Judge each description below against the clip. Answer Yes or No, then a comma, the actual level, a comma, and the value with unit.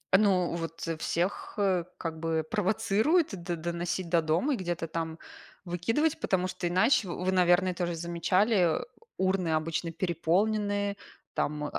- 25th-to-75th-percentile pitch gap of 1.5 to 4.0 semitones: Yes, average, 2.8 semitones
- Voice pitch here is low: No, medium, 175 Hz